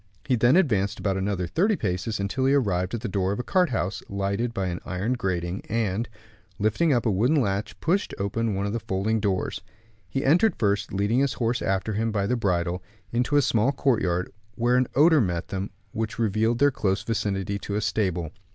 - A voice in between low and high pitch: No, low, 105 Hz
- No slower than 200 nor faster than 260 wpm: Yes, fast, 205 wpm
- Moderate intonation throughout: Yes, average, 4.1 semitones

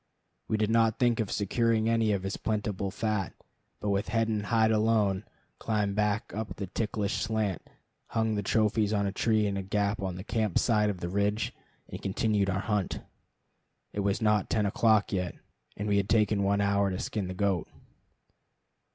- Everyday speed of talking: Yes, average, 185 wpm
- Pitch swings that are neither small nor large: No, narrow, 1.8 semitones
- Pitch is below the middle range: Yes, low, 105 Hz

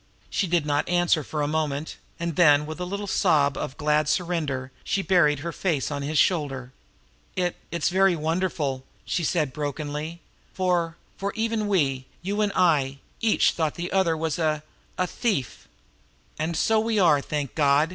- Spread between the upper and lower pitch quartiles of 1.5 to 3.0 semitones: No, average, 3.6 semitones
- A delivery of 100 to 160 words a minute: No, average, 170 wpm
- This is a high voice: No, medium, 160 Hz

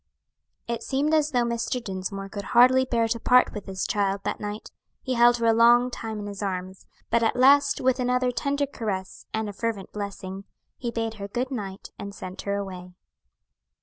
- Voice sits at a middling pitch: No, high, 225 Hz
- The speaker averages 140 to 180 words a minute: No, average, 195 wpm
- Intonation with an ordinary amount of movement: Yes, average, 3.9 semitones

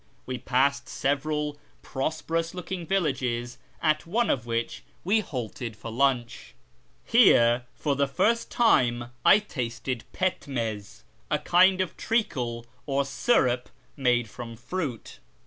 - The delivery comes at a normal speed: No, slow, 120 wpm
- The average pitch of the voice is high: No, low, 135 Hz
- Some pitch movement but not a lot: No, wide, 5.7 semitones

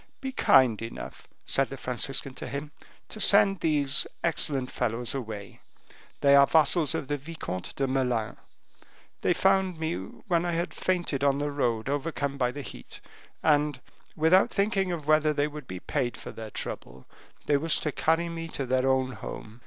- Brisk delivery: No, average, 175 wpm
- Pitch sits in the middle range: Yes, medium, 145 Hz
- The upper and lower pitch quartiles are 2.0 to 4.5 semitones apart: Yes, average, 4.2 semitones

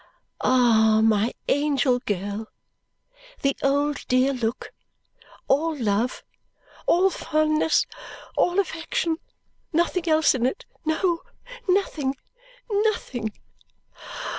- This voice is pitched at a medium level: No, very high, 280 Hz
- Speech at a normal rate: No, slow, 90 wpm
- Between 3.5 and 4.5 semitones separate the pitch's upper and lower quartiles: No, average, 5.3 semitones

